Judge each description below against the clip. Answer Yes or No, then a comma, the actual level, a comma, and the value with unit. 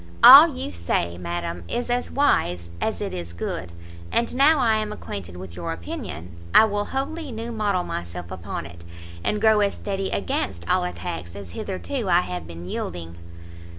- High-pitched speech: No, very low, 90 Hz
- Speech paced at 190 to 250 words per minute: No, average, 175 wpm